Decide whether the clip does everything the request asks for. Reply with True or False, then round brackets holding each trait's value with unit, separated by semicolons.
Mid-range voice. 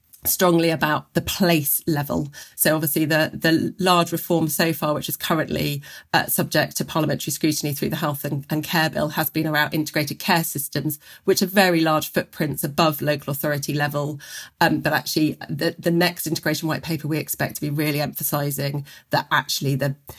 True (155 Hz)